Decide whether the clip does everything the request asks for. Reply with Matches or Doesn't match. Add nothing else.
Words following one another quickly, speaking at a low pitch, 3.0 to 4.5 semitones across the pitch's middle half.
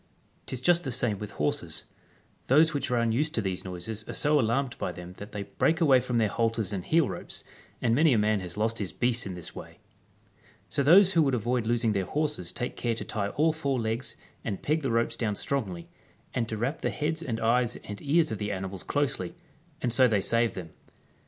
Doesn't match